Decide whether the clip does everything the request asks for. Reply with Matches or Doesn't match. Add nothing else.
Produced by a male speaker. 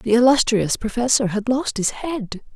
Doesn't match